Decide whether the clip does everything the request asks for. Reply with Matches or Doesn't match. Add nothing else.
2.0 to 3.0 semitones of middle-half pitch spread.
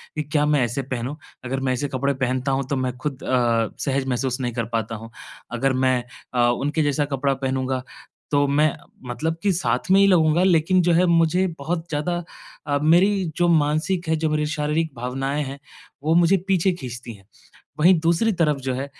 Doesn't match